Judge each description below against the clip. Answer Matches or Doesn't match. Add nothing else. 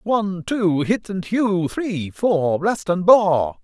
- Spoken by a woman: Doesn't match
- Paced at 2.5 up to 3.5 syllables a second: Matches